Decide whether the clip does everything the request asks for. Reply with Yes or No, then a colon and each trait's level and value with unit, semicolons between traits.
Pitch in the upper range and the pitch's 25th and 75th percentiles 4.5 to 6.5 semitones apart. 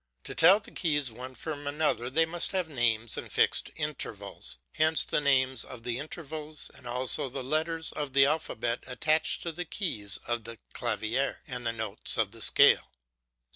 No: low, 135 Hz; average, 4.9 semitones